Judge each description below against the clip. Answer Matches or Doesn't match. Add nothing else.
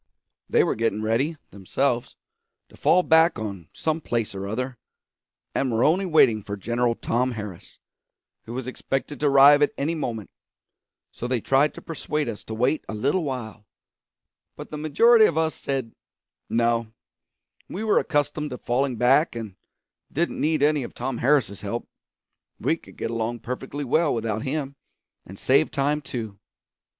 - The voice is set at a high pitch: Doesn't match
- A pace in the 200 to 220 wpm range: Doesn't match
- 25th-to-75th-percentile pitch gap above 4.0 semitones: Matches